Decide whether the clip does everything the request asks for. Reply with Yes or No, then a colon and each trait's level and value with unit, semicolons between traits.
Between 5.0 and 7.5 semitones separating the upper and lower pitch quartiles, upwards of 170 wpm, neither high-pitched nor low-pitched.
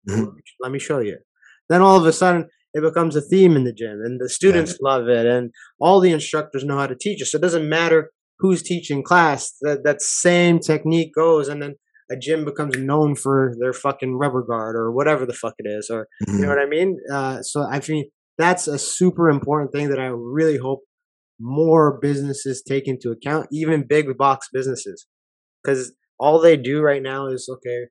No: average, 3.5 semitones; fast, 205 wpm; medium, 145 Hz